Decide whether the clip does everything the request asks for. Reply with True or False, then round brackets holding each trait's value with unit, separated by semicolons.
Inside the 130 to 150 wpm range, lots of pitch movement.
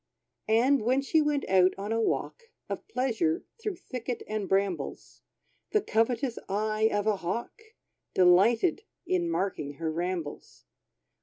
True (135 wpm; 6.8 semitones)